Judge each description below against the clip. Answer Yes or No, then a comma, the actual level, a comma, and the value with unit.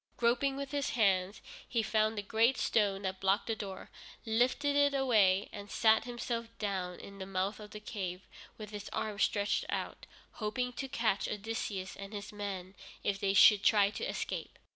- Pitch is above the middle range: Yes, high, 210 Hz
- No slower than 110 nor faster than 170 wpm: No, average, 180 wpm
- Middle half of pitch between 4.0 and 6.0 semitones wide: No, average, 2.9 semitones